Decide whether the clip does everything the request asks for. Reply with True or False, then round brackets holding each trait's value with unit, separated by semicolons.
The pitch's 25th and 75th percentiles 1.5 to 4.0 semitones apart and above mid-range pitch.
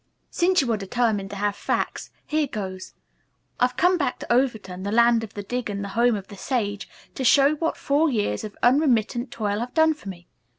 False (5.0 semitones; 235 Hz)